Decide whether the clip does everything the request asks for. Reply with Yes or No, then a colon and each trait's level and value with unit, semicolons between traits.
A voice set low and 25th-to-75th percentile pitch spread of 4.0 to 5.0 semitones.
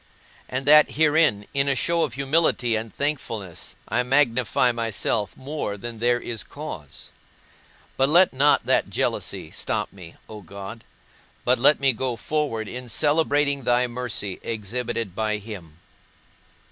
Yes: low, 120 Hz; average, 4.5 semitones